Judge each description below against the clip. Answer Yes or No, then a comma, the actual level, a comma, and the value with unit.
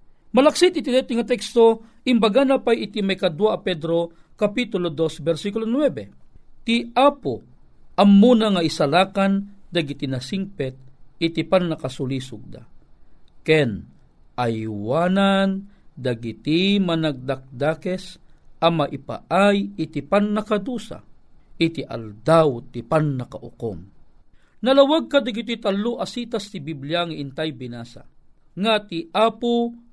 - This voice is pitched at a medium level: Yes, medium, 175 Hz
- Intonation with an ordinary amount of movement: No, wide, 8.0 semitones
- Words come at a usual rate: No, slow, 105 wpm